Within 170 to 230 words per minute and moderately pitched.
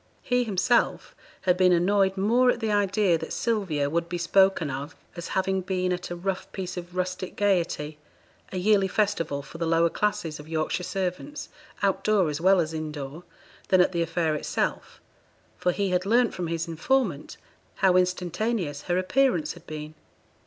Yes: average, 175 wpm; medium, 180 Hz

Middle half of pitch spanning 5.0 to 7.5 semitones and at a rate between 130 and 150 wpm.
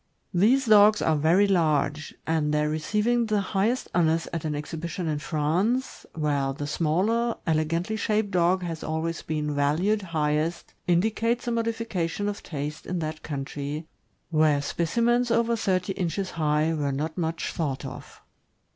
Yes: average, 5.3 semitones; average, 145 wpm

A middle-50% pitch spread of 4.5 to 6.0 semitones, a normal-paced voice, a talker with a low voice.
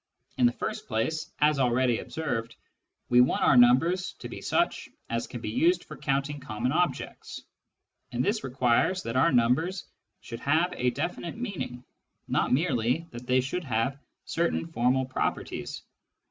Yes: average, 5.3 semitones; average, 155 wpm; low, 130 Hz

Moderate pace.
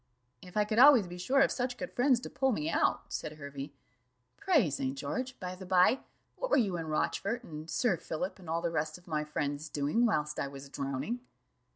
No: fast, 215 wpm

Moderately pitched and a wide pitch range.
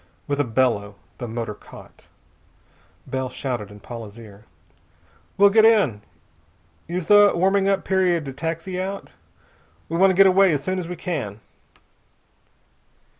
Yes: medium, 165 Hz; wide, 8.2 semitones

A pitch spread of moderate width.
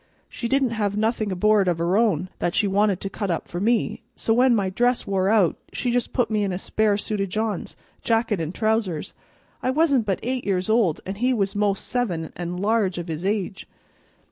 Yes: average, 3.4 semitones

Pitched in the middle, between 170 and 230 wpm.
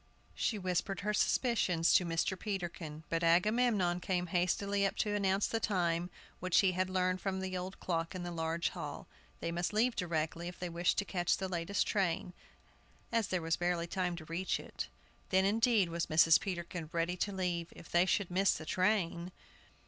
Yes: medium, 180 Hz; average, 185 wpm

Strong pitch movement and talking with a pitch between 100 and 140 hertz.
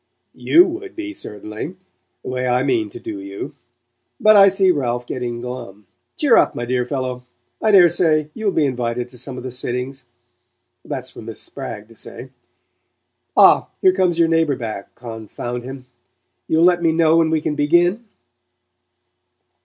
Yes: wide, 6.0 semitones; low, 135 Hz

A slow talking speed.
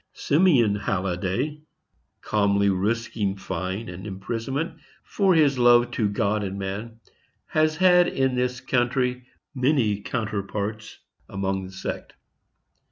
Yes: slow, 110 wpm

